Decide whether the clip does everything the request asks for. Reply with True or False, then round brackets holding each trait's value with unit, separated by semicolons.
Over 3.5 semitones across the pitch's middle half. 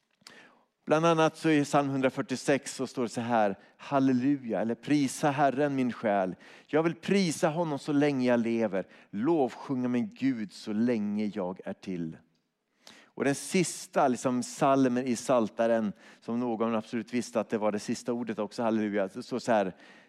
True (4.2 semitones)